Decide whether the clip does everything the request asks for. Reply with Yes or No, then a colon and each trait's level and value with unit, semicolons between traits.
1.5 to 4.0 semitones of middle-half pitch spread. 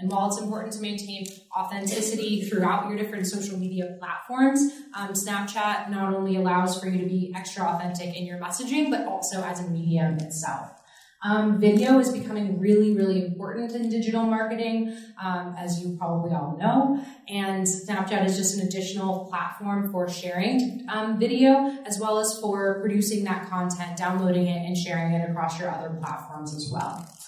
Yes: average, 3.1 semitones